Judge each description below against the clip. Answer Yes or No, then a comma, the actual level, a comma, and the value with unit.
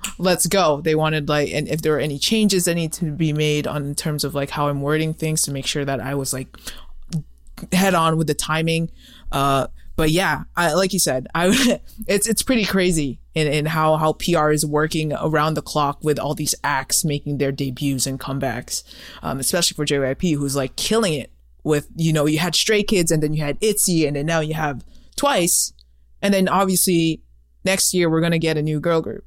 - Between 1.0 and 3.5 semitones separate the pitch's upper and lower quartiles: Yes, average, 3.2 semitones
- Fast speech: Yes, fast, 220 wpm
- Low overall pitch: No, medium, 155 Hz